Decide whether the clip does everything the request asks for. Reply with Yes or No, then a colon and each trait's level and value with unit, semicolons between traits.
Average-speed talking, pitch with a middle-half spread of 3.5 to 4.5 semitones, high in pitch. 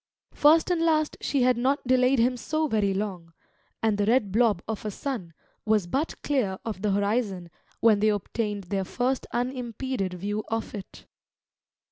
Yes: average, 165 wpm; average, 4.2 semitones; high, 225 Hz